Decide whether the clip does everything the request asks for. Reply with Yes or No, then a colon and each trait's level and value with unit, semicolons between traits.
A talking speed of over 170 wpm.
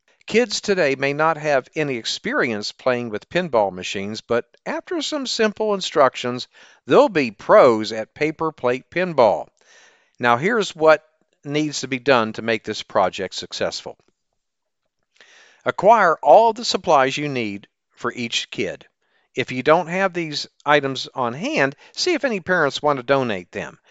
No: average, 150 wpm